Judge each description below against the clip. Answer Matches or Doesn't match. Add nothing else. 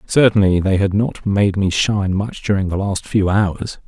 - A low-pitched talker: Matches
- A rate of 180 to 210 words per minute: Matches